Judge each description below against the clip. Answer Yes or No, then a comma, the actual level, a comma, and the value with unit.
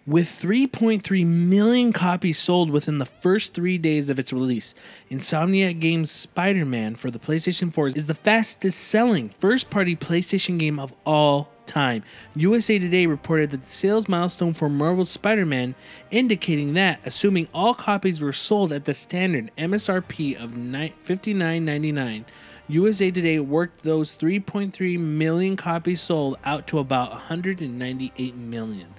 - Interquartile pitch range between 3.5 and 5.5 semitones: Yes, average, 4.9 semitones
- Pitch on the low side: No, medium, 165 Hz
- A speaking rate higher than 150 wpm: No, slow, 135 wpm